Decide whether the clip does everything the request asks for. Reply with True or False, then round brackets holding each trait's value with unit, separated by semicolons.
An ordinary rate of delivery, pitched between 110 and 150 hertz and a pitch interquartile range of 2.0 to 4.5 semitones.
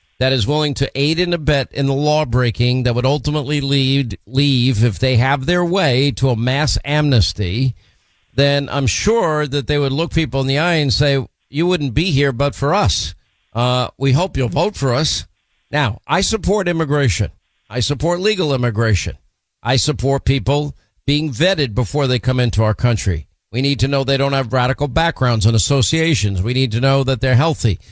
True (190 wpm; 135 Hz; 3.1 semitones)